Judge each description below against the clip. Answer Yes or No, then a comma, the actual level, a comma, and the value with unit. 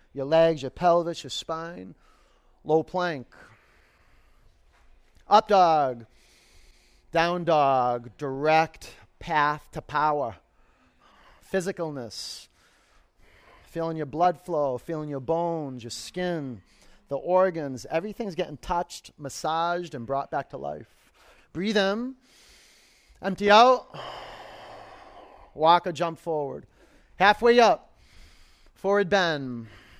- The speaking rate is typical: No, slow, 100 wpm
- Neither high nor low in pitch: Yes, medium, 160 Hz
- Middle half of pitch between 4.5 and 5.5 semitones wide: Yes, average, 5.2 semitones